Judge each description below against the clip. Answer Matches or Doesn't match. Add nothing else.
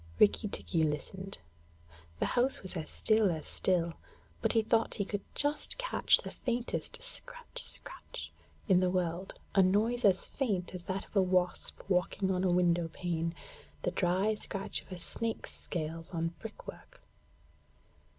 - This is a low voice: Doesn't match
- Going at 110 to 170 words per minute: Matches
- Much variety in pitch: Doesn't match